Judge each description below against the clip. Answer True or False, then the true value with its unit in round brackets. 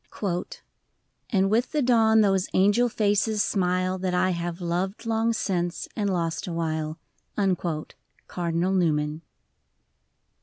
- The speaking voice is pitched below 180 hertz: False (185 Hz)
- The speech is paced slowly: True (115 wpm)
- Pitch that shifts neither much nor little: True (3.8 semitones)